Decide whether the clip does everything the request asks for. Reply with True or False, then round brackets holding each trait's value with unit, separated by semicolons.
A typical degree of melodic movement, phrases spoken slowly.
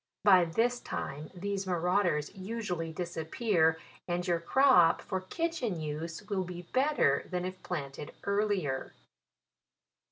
True (3.8 semitones; 120 wpm)